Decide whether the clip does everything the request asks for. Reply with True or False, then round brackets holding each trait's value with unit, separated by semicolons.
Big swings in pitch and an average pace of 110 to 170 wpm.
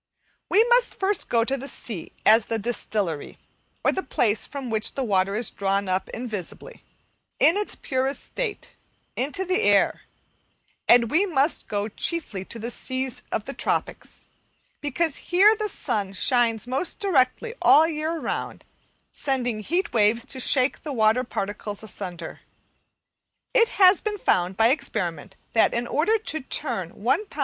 True (7.6 semitones; 155 wpm)